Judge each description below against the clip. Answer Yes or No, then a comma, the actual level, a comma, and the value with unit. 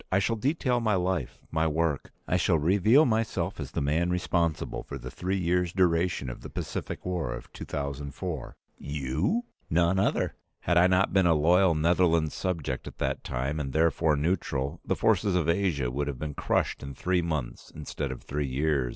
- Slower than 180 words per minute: No, average, 185 wpm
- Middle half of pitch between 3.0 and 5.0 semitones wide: Yes, average, 4.2 semitones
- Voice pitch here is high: No, very low, 85 Hz